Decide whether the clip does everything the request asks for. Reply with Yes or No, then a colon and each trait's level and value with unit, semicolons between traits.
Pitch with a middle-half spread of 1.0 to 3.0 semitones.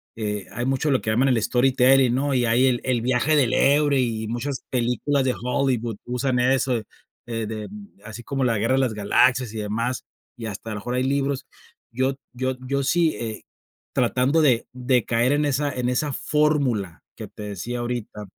Yes: average, 2.7 semitones